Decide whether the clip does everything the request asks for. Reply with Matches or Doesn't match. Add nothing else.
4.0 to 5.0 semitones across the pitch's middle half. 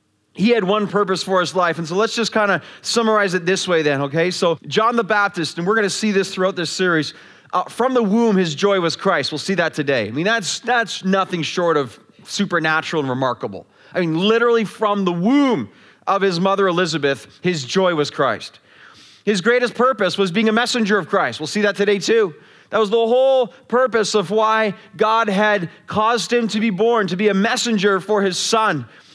Matches